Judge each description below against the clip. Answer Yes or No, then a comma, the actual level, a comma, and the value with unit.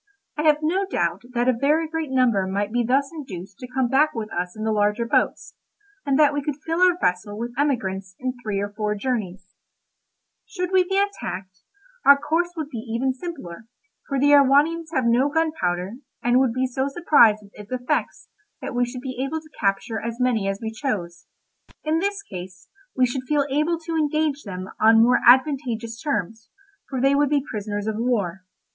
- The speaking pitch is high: Yes, very high, 250 Hz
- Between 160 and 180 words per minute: No, average, 195 wpm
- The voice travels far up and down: Yes, wide, 5.8 semitones